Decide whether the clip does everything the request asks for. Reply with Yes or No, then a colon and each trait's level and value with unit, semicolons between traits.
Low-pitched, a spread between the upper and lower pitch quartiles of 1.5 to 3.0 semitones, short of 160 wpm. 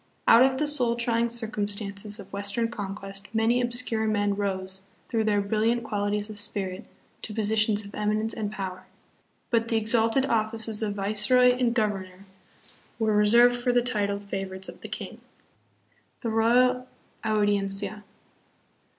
No: high, 215 Hz; narrow, 2.4 semitones; average, 150 wpm